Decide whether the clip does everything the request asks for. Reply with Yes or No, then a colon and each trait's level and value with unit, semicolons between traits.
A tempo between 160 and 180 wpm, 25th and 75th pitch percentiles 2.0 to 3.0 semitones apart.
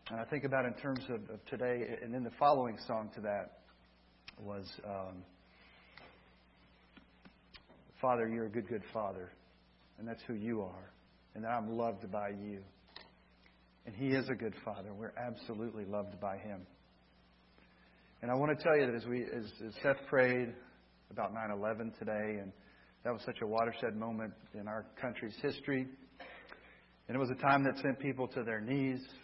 No: average, 170 wpm; average, 4.2 semitones